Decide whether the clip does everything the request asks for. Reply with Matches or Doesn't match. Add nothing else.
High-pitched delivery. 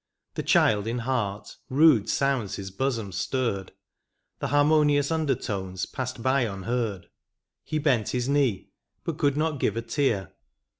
Doesn't match